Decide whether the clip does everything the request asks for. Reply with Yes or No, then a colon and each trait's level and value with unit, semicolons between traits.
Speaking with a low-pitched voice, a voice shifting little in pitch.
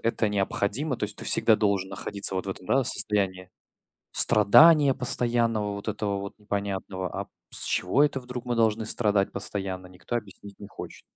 No: low, 105 Hz; average, 3.1 semitones